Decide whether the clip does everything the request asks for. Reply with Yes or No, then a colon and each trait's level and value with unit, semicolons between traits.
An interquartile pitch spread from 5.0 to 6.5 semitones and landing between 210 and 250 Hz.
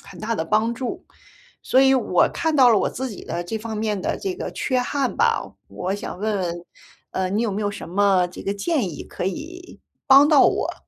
Yes: wide, 5.5 semitones; high, 215 Hz